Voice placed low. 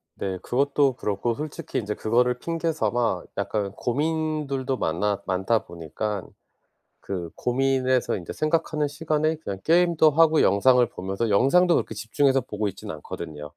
Yes: low, 125 Hz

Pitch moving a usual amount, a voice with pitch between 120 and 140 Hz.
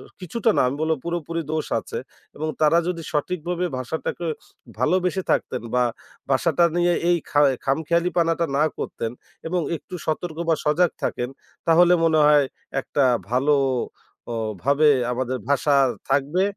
No: average, 3.2 semitones; medium, 160 Hz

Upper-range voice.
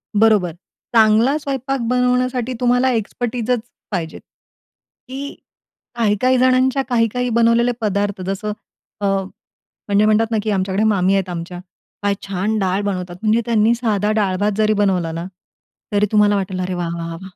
Yes: high, 215 Hz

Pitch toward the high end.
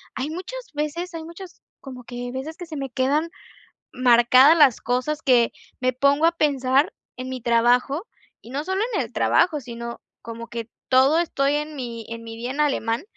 Yes: very high, 265 Hz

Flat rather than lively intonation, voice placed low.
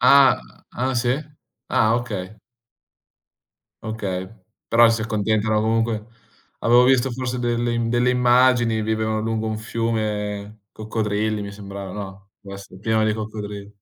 Yes: narrow, 2.3 semitones; low, 110 Hz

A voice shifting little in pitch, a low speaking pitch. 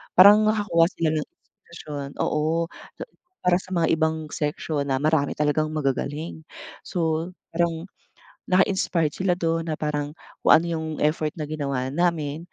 No: narrow, 2.1 semitones; medium, 160 Hz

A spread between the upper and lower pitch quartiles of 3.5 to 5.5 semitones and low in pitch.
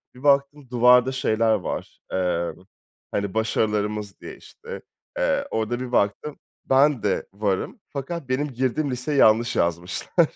Yes: average, 4.7 semitones; low, 120 Hz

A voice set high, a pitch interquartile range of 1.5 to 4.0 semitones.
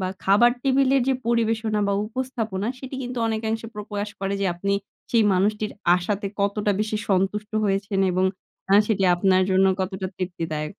Yes: high, 205 Hz; average, 2.8 semitones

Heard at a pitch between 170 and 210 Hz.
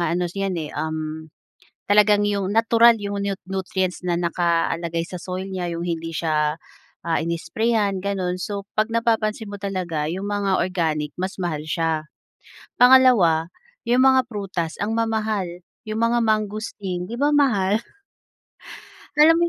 Yes: high, 190 Hz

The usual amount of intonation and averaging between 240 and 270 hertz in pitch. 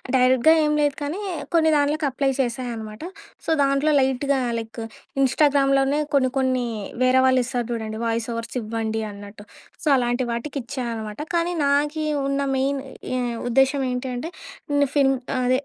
Yes: average, 3.1 semitones; very high, 260 Hz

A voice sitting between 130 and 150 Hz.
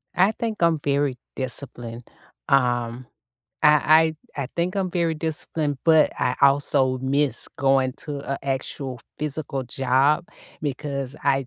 Yes: medium, 140 Hz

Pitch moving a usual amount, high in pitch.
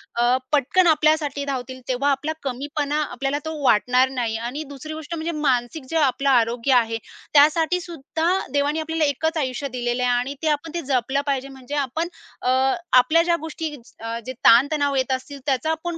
Yes: average, 3.6 semitones; very high, 280 Hz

